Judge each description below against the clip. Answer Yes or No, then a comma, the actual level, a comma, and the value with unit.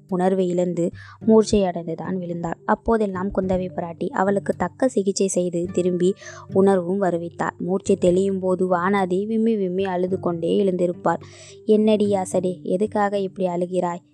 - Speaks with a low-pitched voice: No, medium, 185 Hz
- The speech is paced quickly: No, average, 120 wpm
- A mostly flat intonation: Yes, narrow, 1.9 semitones